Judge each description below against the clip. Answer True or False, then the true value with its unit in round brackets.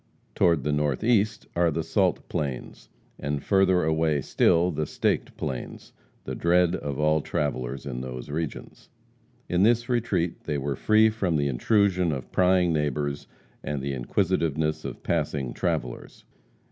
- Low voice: True (80 Hz)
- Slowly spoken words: False (145 wpm)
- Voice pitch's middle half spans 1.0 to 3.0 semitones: False (4.3 semitones)